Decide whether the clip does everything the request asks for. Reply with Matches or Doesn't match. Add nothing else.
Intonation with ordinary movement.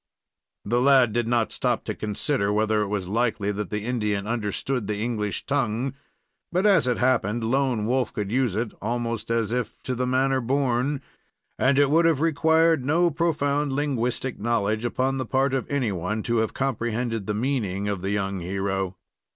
Matches